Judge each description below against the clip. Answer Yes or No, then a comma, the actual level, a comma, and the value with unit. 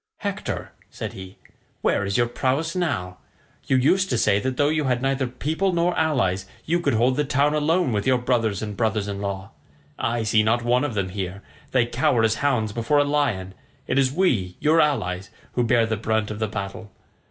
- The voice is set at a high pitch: No, low, 120 Hz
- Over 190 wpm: Yes, fast, 205 wpm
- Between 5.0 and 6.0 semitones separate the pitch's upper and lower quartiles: Yes, wide, 5.6 semitones